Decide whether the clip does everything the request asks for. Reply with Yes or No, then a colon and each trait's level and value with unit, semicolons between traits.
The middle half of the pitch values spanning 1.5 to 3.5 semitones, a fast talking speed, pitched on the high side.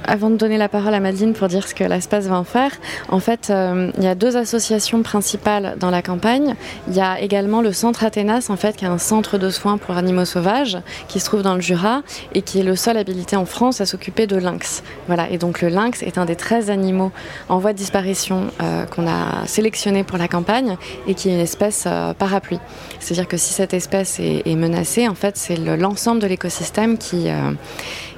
Yes: average, 3.0 semitones; fast, 230 wpm; high, 195 Hz